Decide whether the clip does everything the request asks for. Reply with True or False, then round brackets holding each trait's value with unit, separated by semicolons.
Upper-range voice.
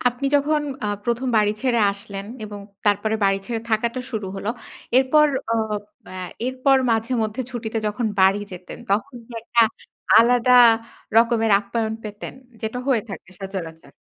True (225 Hz)